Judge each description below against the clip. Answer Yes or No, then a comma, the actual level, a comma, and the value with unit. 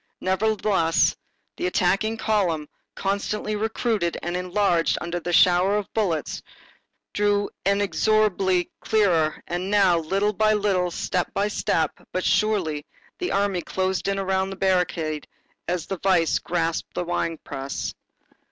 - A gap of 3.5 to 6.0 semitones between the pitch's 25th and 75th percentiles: No, average, 3.0 semitones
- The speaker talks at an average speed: No, slow, 130 wpm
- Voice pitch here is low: No, high, 190 Hz